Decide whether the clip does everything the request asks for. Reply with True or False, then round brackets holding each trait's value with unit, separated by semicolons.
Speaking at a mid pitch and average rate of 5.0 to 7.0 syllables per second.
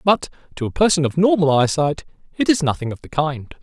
True (160 Hz; 5.7 syllables/s)